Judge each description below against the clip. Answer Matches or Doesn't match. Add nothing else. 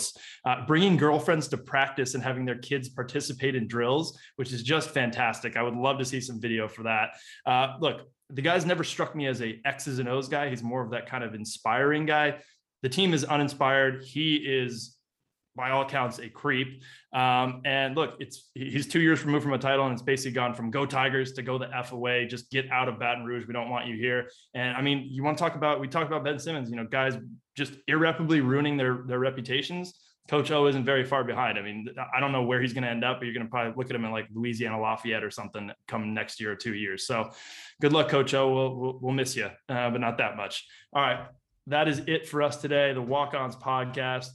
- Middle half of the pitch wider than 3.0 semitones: Doesn't match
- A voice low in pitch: Matches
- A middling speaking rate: Doesn't match